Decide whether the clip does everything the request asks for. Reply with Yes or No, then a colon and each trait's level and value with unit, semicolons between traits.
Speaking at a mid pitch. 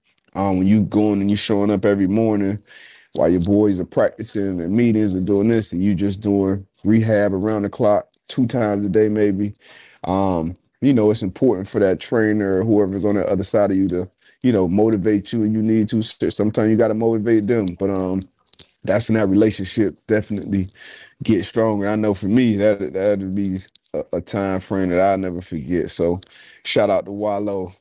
No: low, 100 Hz